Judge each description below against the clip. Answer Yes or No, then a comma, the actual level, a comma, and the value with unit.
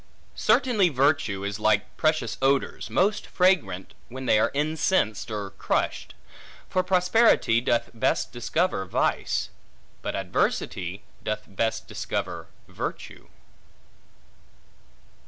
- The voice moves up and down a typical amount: No, wide, 8.9 semitones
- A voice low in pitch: Yes, low, 125 Hz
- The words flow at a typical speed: No, slow, 100 wpm